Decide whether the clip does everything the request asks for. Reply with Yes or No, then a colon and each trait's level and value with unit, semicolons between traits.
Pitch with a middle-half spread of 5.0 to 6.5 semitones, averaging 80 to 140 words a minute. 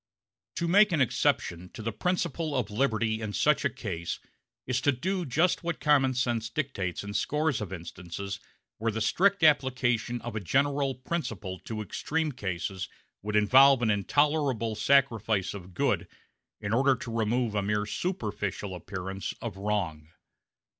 No: wide, 5.4 semitones; average, 155 wpm